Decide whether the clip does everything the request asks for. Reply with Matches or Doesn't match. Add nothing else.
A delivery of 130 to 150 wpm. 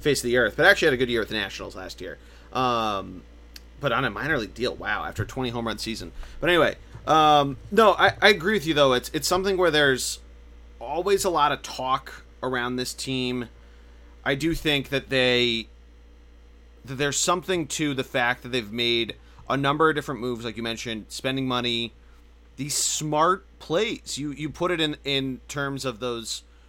Doesn't match